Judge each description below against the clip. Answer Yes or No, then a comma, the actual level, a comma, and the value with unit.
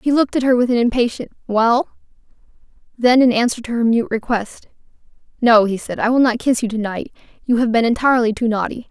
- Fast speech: Yes, fast, 210 wpm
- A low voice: No, high, 235 Hz